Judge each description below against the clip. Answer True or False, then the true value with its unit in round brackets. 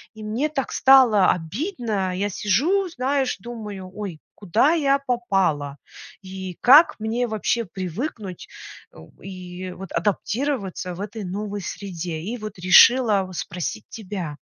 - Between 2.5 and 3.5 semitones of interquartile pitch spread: False (4.9 semitones)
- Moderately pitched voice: False (205 Hz)